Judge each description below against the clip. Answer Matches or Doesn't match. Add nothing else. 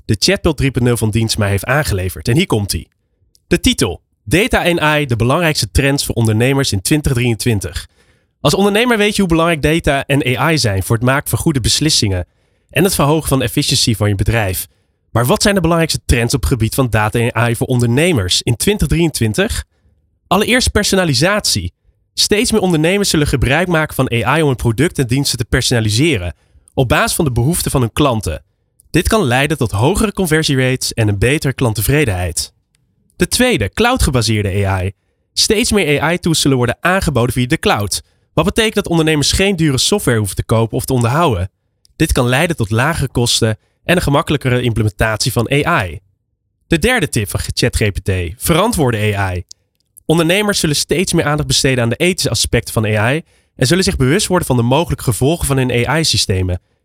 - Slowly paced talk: Doesn't match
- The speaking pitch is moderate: Doesn't match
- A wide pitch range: Matches